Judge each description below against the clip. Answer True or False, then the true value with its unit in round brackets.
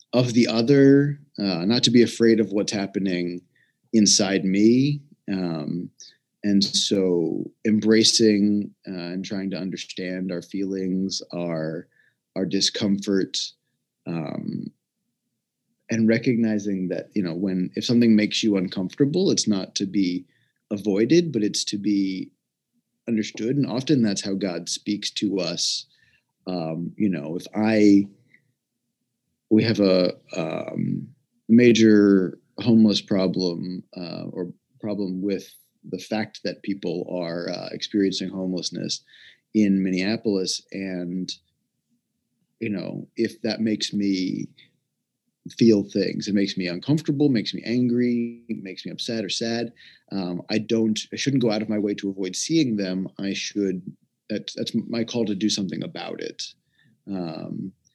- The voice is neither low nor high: False (100 Hz)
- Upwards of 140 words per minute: False (135 wpm)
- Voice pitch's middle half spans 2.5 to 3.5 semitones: True (3.1 semitones)